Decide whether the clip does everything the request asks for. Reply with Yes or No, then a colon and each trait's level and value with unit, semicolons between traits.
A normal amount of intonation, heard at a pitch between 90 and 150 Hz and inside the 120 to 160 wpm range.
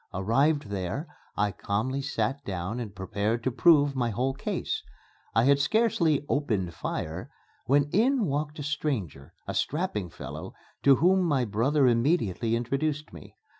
No: wide, 6.2 semitones; low, 135 Hz; average, 145 wpm